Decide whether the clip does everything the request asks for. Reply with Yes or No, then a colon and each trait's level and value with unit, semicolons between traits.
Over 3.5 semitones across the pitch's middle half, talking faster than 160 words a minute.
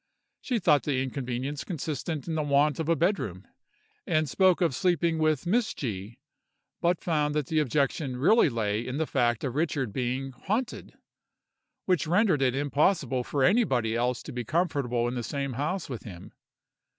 Yes: average, 4.9 semitones; average, 175 wpm